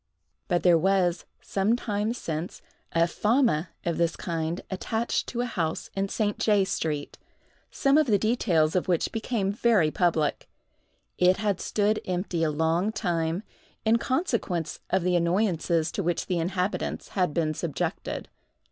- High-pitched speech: No, medium, 180 Hz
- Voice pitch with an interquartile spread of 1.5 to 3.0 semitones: No, average, 4.1 semitones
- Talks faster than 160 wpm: No, average, 150 wpm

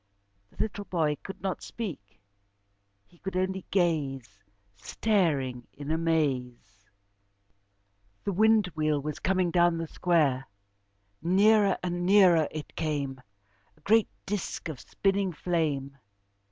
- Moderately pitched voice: Yes, medium, 165 Hz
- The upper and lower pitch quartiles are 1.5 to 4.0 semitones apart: No, average, 5.0 semitones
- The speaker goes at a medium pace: No, slow, 115 wpm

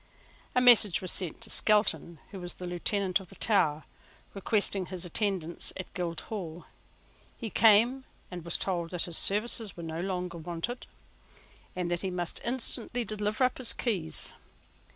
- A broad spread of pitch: No, average, 3.8 semitones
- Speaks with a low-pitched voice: No, medium, 185 Hz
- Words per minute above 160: No, average, 155 wpm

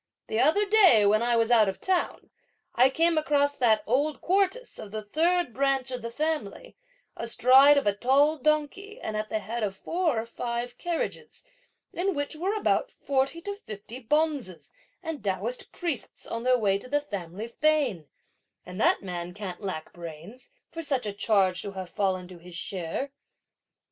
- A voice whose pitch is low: No, high, 245 Hz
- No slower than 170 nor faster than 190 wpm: Yes, average, 175 wpm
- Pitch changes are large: Yes, wide, 7.0 semitones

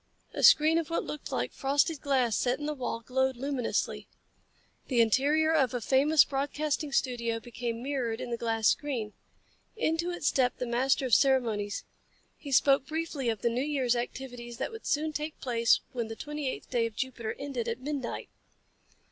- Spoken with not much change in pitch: No, average, 3.7 semitones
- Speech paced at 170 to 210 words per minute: Yes, average, 180 wpm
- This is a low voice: No, very high, 260 Hz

